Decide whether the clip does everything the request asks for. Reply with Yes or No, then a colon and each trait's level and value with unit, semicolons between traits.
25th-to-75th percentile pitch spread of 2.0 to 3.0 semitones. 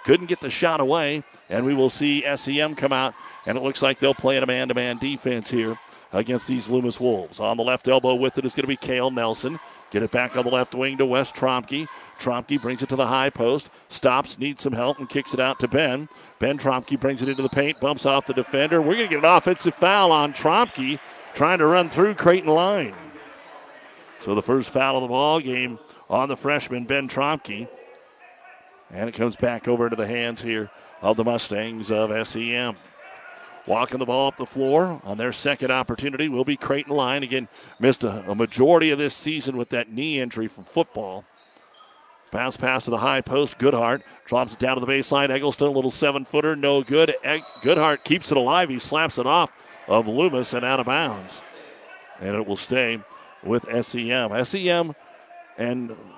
Yes: average, 2.7 semitones